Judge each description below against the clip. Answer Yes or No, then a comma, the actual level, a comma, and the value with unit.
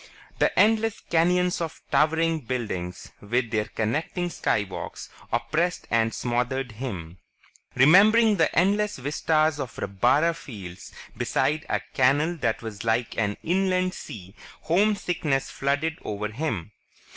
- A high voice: No, medium, 140 Hz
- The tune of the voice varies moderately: No, wide, 7.4 semitones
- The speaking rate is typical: No, slow, 120 wpm